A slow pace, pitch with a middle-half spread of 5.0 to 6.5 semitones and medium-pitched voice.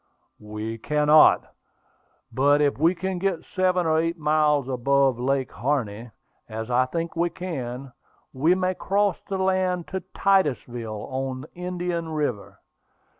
Yes: slow, 130 wpm; wide, 5.6 semitones; medium, 150 Hz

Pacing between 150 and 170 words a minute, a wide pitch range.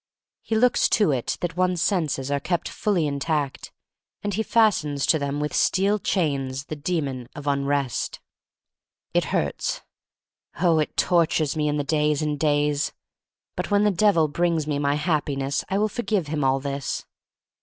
No: average, 165 wpm; average, 4.2 semitones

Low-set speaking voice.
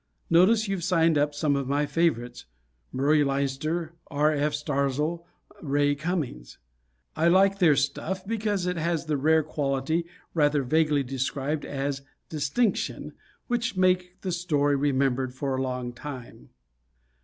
No: medium, 150 Hz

